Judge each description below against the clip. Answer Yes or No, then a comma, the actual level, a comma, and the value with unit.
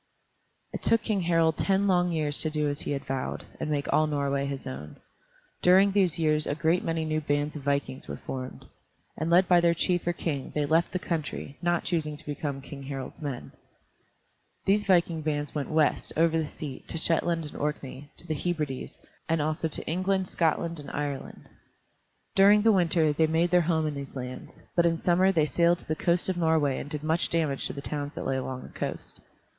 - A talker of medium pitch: Yes, medium, 155 Hz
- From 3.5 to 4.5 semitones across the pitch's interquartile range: No, average, 3.0 semitones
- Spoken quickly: Yes, fast, 210 wpm